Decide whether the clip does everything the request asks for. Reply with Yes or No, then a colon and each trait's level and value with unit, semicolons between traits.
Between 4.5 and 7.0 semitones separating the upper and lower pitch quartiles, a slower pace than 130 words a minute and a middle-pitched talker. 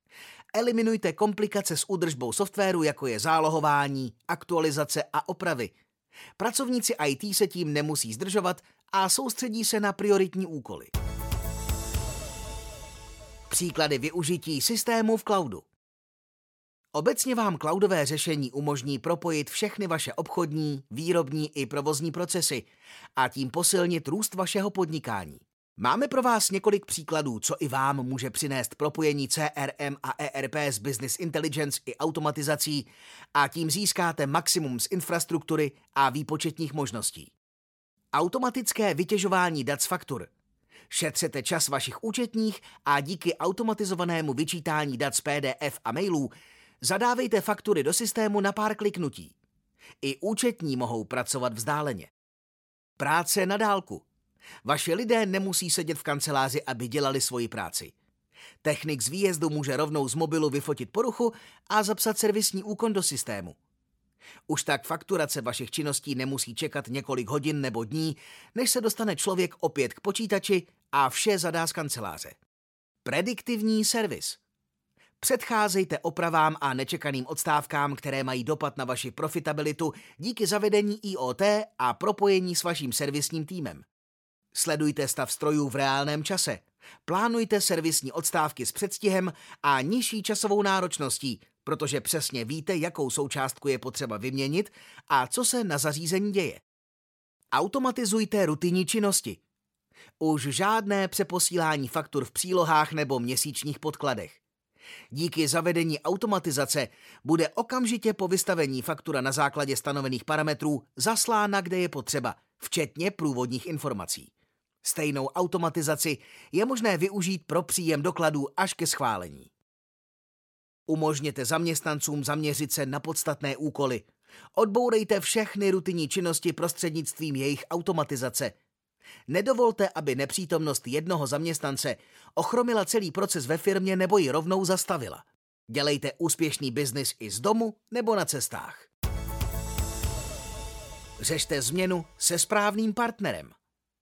Yes: wide, 5.6 semitones; average, 120 wpm; medium, 160 Hz